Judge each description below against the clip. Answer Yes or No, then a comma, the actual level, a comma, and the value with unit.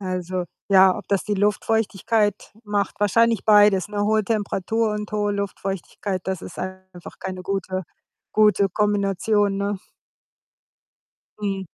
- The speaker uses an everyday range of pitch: No, narrow, 1.8 semitones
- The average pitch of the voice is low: No, high, 200 Hz